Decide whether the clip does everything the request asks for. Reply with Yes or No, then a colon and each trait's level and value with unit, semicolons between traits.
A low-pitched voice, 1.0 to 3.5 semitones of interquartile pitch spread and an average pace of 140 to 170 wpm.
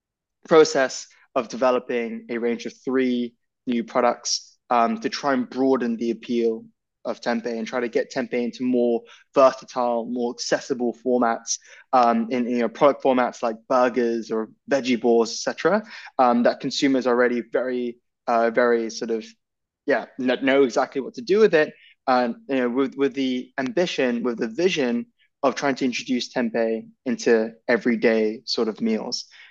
Yes: low, 125 Hz; narrow, 2.4 semitones; average, 165 wpm